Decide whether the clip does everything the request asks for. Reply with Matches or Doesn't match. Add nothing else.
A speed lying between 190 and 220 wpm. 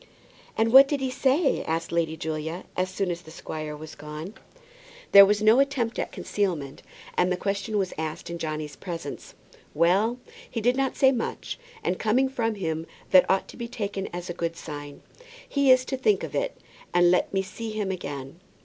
Matches